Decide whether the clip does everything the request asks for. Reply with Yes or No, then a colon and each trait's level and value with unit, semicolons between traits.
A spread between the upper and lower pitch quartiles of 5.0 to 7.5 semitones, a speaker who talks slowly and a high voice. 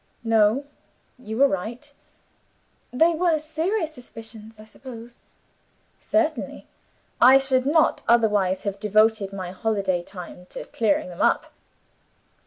Yes: average, 5.3 semitones; slow, 115 wpm; high, 225 Hz